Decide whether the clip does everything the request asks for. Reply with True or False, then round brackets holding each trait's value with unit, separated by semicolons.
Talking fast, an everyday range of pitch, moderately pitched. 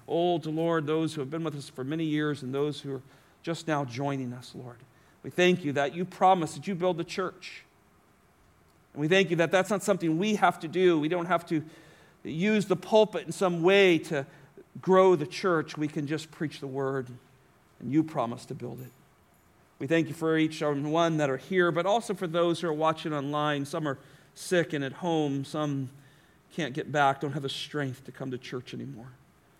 True (215 wpm; 3.5 semitones; 155 Hz)